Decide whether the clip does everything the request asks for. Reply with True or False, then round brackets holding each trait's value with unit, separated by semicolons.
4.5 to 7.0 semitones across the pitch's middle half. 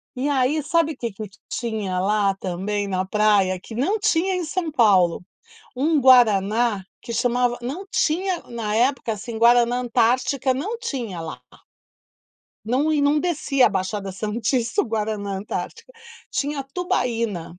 True (5.5 semitones)